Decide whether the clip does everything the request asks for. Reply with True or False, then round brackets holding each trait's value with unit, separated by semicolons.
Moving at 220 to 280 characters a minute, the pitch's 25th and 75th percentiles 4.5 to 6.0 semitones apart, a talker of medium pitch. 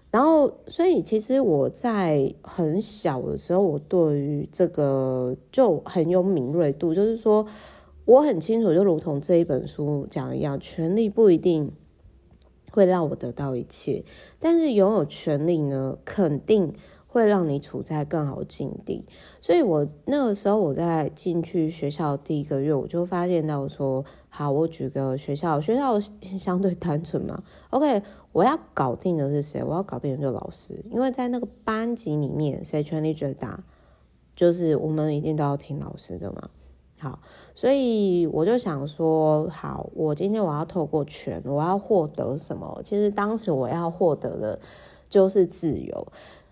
True (245 characters per minute; 5.5 semitones; 165 Hz)